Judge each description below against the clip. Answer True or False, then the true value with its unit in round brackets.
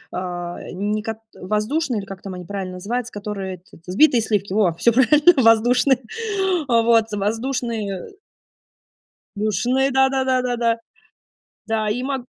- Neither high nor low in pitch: False (225 Hz)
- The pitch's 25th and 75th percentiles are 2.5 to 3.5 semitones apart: False (4.3 semitones)